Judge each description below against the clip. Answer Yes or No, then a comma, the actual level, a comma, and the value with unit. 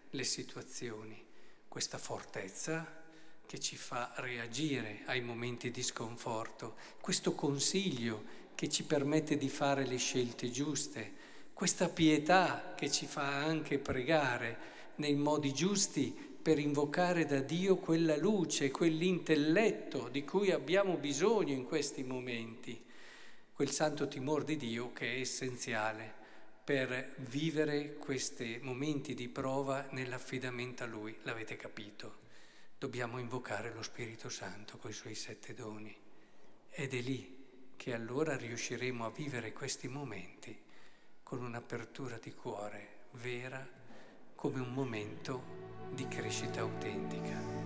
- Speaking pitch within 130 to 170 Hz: Yes, low, 135 Hz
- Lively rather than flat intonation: No, average, 3.6 semitones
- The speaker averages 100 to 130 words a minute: Yes, average, 120 wpm